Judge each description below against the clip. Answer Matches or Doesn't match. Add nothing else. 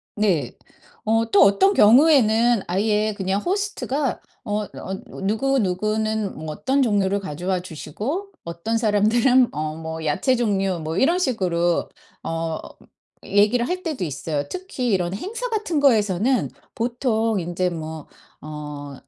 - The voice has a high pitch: Matches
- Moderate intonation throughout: Doesn't match